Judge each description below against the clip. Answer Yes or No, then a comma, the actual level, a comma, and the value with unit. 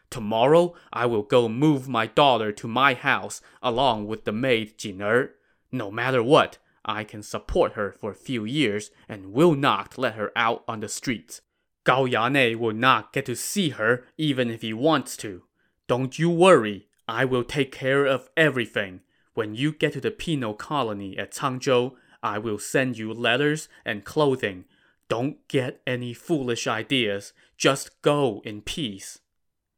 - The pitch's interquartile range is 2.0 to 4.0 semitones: No, average, 4.6 semitones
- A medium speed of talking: Yes, average, 165 wpm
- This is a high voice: No, low, 120 Hz